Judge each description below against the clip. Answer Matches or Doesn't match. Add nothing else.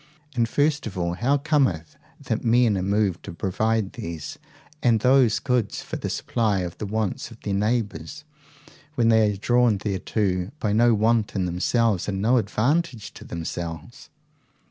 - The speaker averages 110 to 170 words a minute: Matches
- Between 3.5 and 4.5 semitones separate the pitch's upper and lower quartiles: Matches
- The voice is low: Matches